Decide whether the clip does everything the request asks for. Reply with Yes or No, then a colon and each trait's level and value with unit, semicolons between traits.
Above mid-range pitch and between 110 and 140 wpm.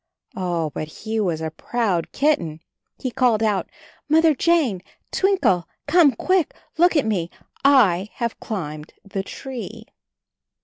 Yes: high, 220 Hz; slow, 135 wpm